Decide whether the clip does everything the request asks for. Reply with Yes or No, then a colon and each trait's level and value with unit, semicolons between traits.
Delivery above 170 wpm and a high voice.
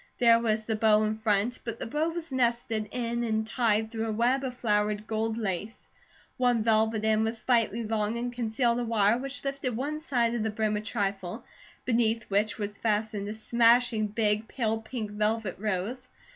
Yes: average, 185 wpm; high, 225 Hz